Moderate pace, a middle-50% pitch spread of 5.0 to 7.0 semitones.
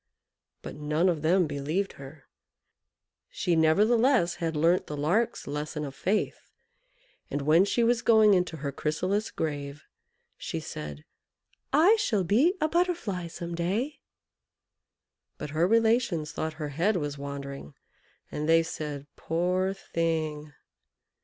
No: slow, 130 wpm; wide, 5.6 semitones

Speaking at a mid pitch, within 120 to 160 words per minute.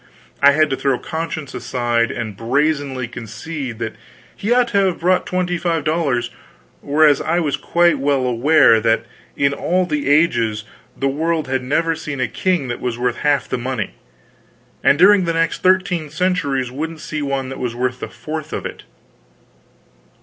No: medium, 145 Hz; average, 170 wpm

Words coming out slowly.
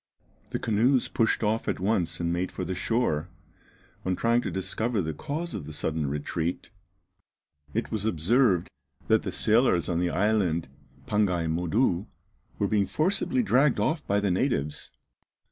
No: average, 155 wpm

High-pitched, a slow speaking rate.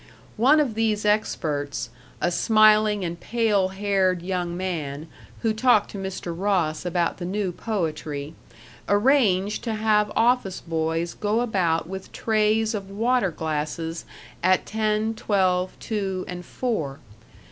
Yes: high, 195 Hz; slow, 130 wpm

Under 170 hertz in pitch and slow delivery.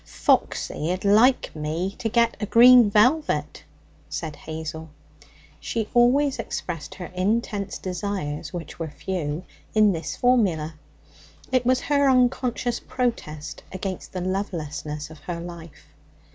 No: high, 190 Hz; slow, 120 wpm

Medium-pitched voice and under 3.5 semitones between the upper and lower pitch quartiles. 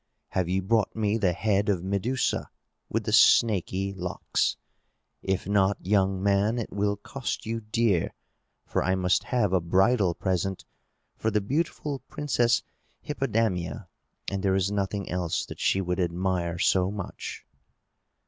No: low, 100 Hz; average, 2.7 semitones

